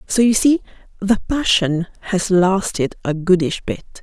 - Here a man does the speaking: No, female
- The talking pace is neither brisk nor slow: Yes, average, 150 wpm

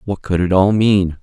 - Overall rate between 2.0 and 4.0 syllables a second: No, 4.6 syllables/s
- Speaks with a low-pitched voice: Yes, very low, 95 Hz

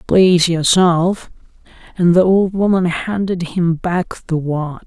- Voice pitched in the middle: Yes, medium, 175 Hz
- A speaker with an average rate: No, slow, 125 wpm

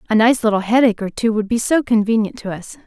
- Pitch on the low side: No, high, 225 Hz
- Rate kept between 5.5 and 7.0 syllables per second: Yes, 6.5 syllables/s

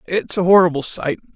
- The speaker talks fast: No, average, 175 wpm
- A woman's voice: Yes, female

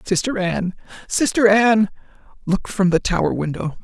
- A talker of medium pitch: Yes, medium, 180 Hz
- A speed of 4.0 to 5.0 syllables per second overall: No, 5.3 syllables/s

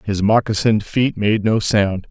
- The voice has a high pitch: No, low, 105 Hz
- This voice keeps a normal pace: Yes, average, 170 wpm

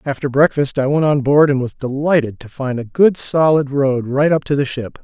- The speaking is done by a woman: No, male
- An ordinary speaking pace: No, fast, 240 wpm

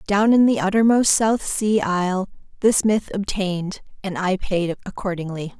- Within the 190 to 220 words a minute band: No, average, 150 wpm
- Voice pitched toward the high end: Yes, high, 195 Hz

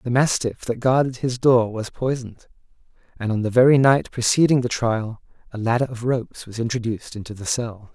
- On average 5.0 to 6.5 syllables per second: Yes, 5.6 syllables/s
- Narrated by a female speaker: No, male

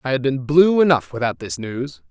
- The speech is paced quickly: Yes, fast, 230 wpm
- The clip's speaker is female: No, male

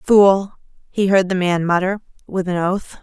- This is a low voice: No, high, 190 Hz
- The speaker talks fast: No, average, 180 wpm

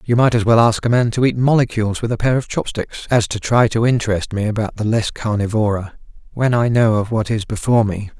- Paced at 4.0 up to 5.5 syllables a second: No, 6.0 syllables/s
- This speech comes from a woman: No, male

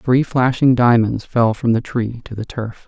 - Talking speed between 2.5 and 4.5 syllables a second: Yes, 4.3 syllables/s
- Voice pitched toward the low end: Yes, low, 120 Hz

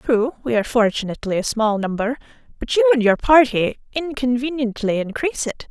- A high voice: Yes, high, 245 Hz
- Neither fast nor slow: Yes, average, 160 wpm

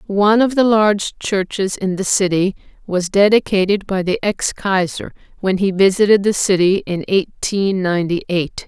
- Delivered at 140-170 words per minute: Yes, average, 160 wpm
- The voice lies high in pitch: Yes, high, 195 Hz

